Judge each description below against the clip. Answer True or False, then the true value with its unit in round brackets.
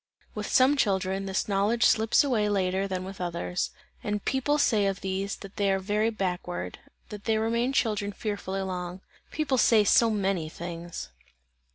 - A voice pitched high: True (200 Hz)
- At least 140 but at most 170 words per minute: True (165 wpm)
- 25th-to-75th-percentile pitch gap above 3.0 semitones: False (2.7 semitones)